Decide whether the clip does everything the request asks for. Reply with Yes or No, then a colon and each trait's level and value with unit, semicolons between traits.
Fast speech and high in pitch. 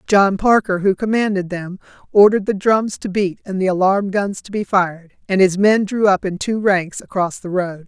Yes: fast, 215 wpm; high, 195 Hz